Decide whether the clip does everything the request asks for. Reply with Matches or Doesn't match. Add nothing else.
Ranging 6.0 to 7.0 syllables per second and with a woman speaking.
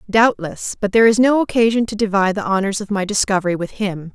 Matches